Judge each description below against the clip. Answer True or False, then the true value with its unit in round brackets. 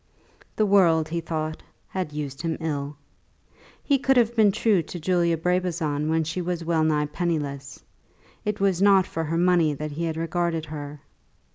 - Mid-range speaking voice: True (165 Hz)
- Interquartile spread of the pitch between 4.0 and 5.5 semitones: False (2.8 semitones)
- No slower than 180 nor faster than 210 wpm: False (170 wpm)